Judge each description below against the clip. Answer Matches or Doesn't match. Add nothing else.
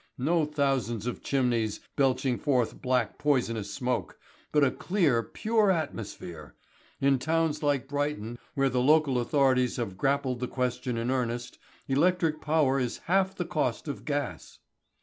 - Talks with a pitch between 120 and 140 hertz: Matches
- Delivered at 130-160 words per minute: Matches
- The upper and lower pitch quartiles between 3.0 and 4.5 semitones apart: Matches